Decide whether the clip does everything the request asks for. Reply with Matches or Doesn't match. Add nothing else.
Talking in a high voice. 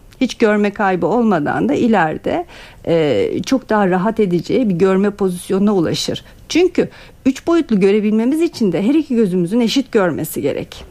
Matches